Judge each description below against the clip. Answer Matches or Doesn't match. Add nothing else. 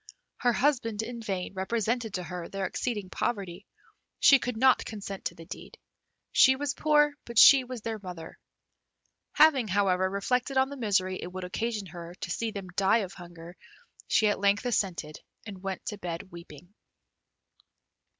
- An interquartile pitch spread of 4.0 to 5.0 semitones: Matches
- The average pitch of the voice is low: Doesn't match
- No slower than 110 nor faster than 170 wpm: Matches